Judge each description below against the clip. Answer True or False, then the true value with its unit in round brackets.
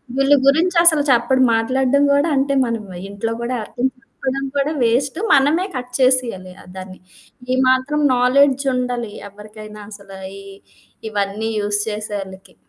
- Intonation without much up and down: False (4.4 semitones)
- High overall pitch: True (250 Hz)